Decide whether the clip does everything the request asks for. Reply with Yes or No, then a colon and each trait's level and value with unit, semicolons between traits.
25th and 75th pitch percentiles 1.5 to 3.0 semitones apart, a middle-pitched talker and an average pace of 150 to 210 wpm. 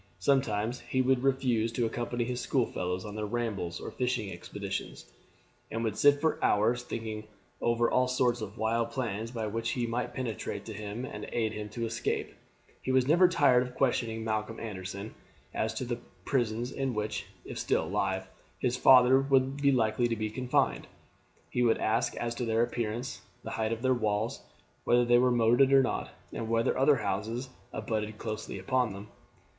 No: average, 2.7 semitones; low, 115 Hz; average, 185 wpm